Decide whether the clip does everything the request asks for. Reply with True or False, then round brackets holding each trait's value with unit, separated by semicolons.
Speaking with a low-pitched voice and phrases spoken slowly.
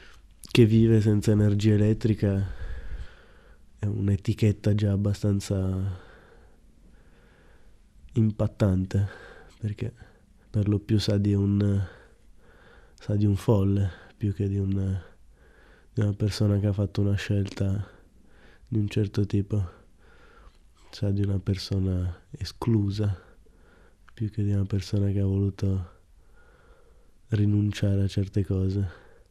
True (100 Hz; 110 wpm)